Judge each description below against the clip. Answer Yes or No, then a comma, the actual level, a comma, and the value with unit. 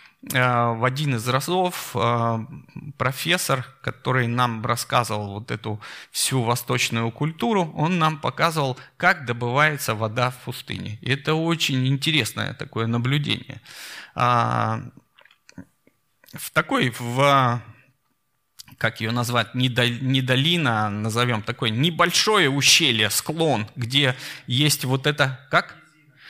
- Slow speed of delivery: Yes, slow, 105 wpm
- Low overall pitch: Yes, low, 130 Hz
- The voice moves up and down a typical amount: Yes, average, 3.8 semitones